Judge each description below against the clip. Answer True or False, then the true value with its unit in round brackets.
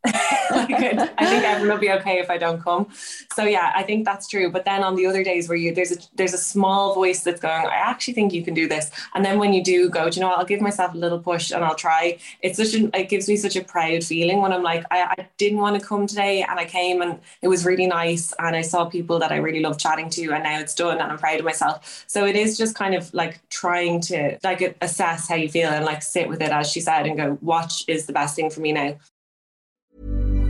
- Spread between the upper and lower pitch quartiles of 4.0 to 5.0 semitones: False (3.1 semitones)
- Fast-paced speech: True (275 wpm)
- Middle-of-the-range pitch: True (175 Hz)